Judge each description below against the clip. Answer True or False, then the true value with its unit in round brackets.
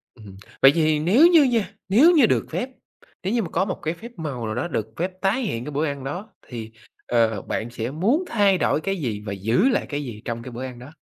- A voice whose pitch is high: False (155 Hz)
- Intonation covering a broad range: True (8.8 semitones)